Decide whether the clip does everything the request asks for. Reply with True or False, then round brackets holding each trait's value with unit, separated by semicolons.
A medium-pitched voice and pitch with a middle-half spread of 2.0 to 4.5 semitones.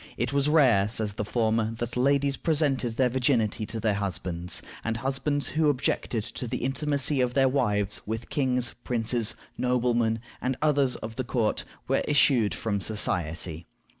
False (120 Hz; 3.7 semitones)